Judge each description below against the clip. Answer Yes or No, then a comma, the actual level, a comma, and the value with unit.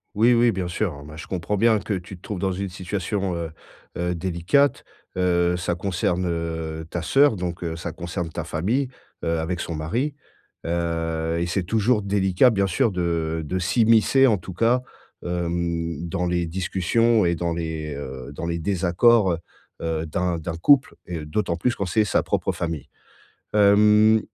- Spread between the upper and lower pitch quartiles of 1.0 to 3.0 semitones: No, average, 3.7 semitones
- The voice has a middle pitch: No, very low, 90 Hz